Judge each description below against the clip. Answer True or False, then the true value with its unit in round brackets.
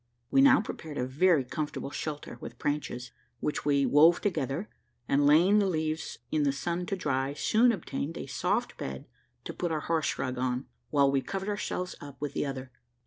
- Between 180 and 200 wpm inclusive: True (190 wpm)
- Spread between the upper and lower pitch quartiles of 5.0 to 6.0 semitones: False (4.2 semitones)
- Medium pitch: True (150 Hz)